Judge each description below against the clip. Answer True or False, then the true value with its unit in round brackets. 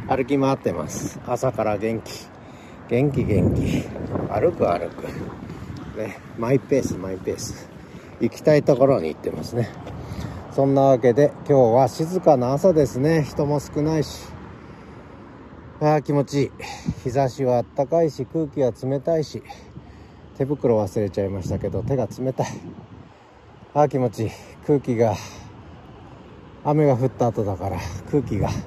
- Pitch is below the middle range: True (125 Hz)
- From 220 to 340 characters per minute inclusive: True (270 characters per minute)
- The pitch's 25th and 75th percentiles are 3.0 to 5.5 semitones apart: True (5.2 semitones)